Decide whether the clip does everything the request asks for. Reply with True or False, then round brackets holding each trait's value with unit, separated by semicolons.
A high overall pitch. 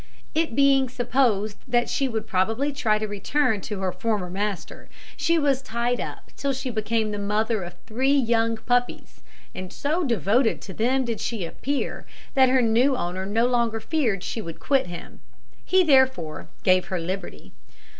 True (230 Hz)